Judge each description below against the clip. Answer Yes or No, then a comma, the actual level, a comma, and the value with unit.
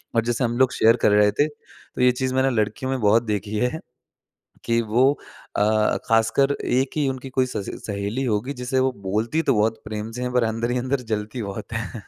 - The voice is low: Yes, low, 115 Hz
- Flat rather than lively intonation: No, average, 3.2 semitones